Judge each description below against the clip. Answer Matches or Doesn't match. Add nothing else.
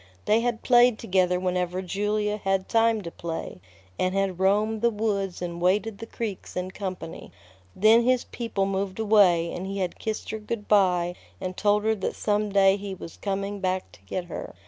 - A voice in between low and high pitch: Doesn't match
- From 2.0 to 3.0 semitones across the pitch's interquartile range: Matches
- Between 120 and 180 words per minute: Doesn't match